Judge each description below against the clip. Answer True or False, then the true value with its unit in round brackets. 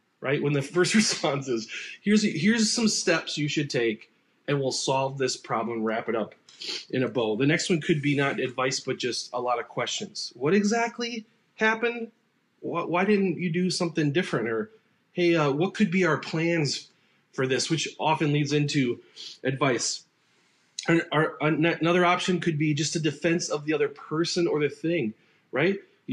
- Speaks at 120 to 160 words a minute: False (180 wpm)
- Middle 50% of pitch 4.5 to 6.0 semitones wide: True (5.0 semitones)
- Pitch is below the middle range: False (170 Hz)